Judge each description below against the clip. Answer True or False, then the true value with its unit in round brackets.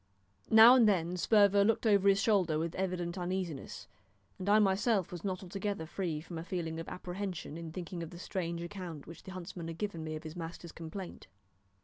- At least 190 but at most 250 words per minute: True (200 wpm)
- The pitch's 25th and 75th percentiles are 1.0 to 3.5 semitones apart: True (3.0 semitones)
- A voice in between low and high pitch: True (180 Hz)